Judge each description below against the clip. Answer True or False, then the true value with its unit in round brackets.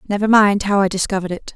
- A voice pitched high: True (200 Hz)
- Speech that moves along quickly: True (230 wpm)